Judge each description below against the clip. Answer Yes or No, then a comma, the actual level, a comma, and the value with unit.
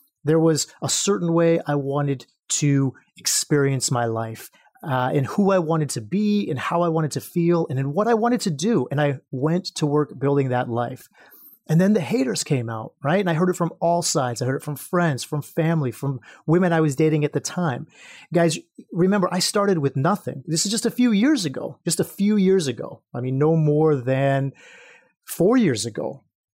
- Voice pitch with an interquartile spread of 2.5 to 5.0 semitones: Yes, average, 4.6 semitones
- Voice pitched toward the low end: No, medium, 160 Hz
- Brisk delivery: Yes, fast, 215 wpm